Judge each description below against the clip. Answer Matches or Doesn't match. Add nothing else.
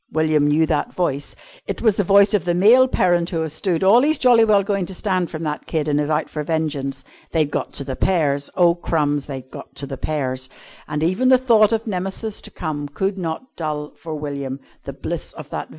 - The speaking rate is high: Matches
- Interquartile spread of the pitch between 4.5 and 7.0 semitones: Matches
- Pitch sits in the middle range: Matches